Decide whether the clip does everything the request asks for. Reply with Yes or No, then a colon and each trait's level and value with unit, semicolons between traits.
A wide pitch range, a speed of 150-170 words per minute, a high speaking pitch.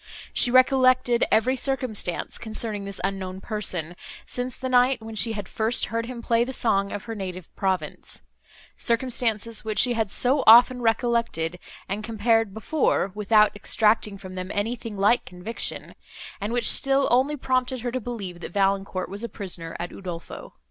No: average, 3.8 semitones; average, 160 wpm; high, 220 Hz